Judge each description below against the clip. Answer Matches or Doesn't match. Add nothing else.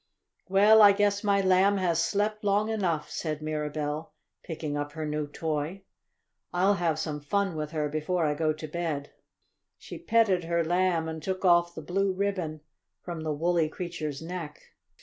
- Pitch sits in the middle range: Matches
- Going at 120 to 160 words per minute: Doesn't match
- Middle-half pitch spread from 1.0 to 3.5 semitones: Doesn't match